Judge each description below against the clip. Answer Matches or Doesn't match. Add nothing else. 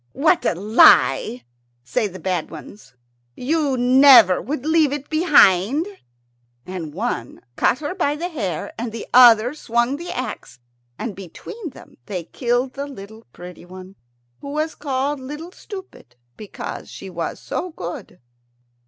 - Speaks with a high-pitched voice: Matches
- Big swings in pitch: Matches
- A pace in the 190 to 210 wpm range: Doesn't match